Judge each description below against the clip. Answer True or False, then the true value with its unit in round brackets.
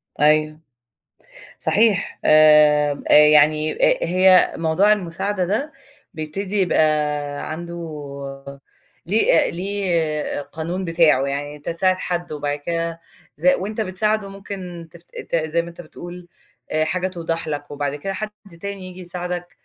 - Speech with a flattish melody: False (3.3 semitones)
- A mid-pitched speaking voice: True (170 Hz)